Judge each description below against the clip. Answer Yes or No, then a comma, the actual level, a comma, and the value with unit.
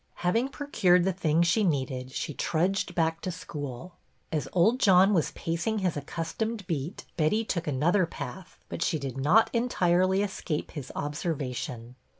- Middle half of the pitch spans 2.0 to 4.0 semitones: No, average, 4.4 semitones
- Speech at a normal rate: Yes, average, 155 wpm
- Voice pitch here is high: No, medium, 170 Hz